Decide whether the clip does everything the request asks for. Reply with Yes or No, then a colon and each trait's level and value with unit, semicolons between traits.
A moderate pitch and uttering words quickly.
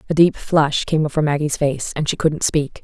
Yes: medium, 150 Hz; fast, 235 wpm